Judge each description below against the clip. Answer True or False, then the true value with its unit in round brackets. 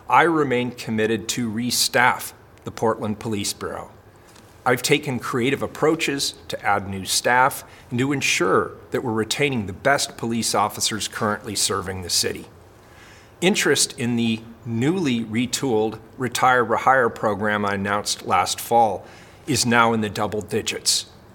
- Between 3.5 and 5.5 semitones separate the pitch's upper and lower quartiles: False (2.4 semitones)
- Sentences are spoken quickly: False (140 wpm)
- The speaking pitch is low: True (115 Hz)